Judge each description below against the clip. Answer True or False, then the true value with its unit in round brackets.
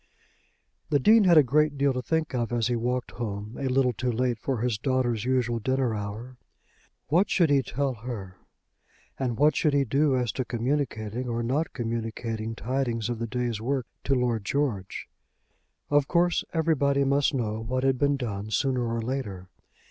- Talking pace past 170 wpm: True (180 wpm)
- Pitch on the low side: True (125 Hz)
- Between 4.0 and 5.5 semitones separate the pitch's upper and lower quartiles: False (3.3 semitones)